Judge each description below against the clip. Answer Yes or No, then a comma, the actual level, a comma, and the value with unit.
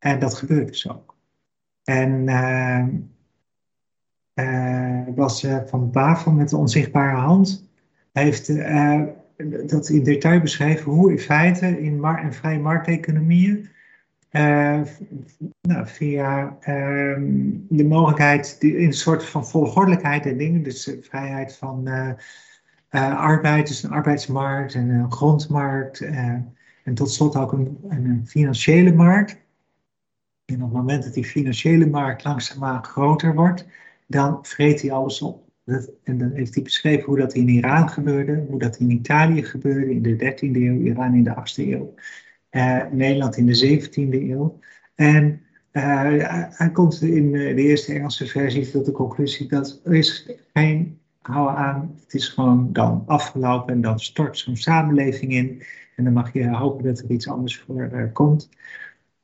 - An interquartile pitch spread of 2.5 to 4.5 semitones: Yes, average, 2.8 semitones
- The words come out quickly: No, average, 155 wpm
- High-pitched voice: No, medium, 140 Hz